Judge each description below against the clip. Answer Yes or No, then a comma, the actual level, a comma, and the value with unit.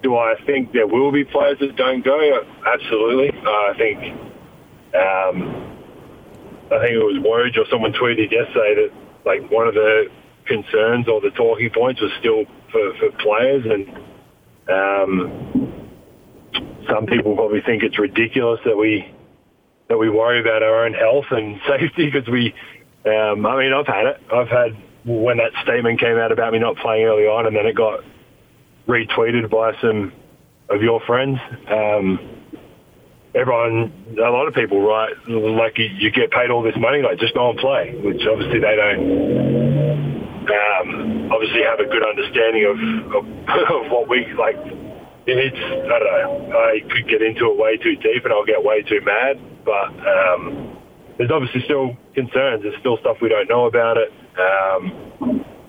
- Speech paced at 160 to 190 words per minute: Yes, average, 170 wpm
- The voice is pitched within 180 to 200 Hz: No, low, 135 Hz